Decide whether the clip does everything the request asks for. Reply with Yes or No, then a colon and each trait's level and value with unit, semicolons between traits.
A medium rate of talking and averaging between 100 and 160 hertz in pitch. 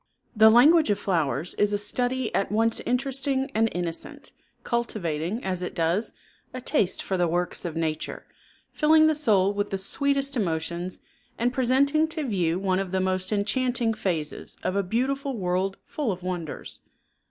No: average, 165 wpm; high, 205 Hz